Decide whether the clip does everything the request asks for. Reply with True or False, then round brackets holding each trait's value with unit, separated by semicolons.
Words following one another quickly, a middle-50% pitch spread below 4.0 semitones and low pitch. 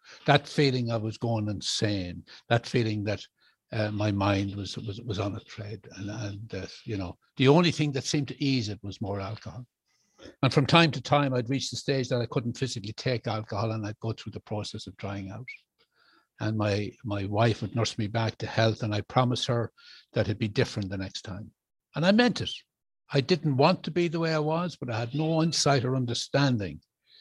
False (220 wpm; 4.8 semitones; 115 Hz)